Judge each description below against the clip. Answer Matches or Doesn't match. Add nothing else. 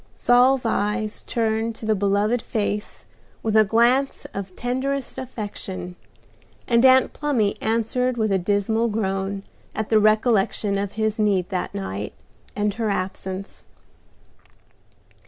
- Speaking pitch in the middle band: Doesn't match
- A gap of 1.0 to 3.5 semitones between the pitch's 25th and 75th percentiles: Matches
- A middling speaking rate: Doesn't match